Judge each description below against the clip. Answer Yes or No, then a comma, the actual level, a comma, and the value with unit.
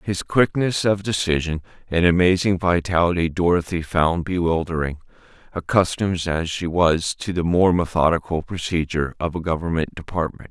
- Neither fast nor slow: No, slow, 130 wpm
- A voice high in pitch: No, very low, 85 Hz